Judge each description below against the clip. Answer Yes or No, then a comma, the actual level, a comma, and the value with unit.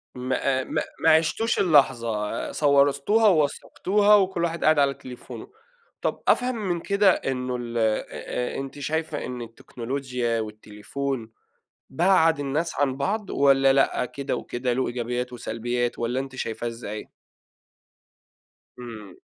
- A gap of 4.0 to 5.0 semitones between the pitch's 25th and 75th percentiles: Yes, average, 4.6 semitones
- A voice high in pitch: No, low, 135 Hz